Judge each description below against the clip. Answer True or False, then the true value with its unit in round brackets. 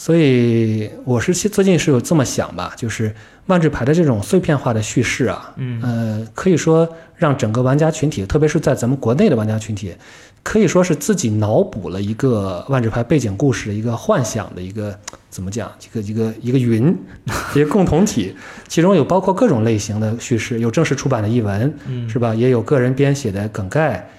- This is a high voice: False (125 Hz)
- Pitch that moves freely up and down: True (5.9 semitones)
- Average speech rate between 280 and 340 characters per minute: True (305 characters per minute)